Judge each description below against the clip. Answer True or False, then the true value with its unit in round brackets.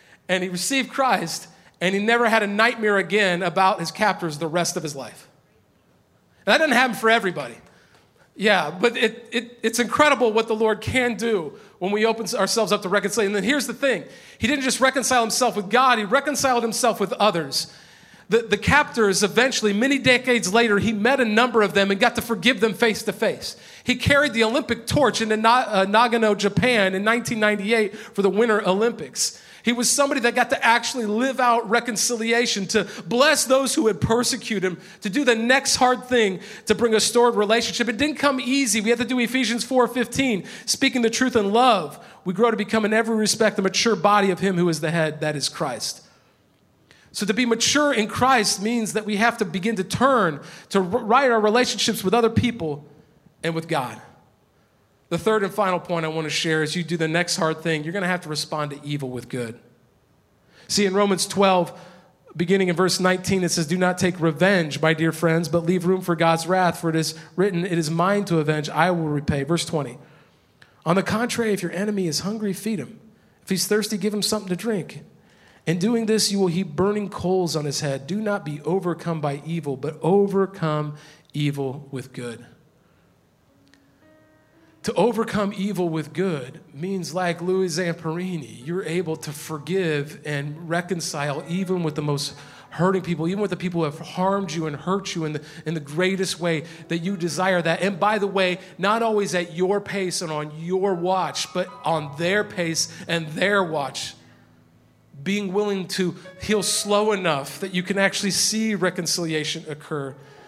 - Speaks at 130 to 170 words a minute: False (195 wpm)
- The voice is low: False (195 Hz)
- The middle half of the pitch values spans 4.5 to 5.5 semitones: True (5.2 semitones)